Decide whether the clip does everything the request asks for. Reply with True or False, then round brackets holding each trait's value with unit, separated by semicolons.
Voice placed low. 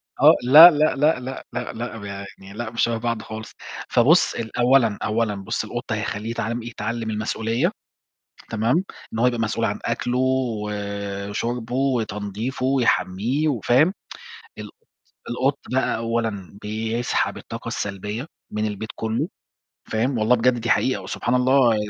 True (115 Hz)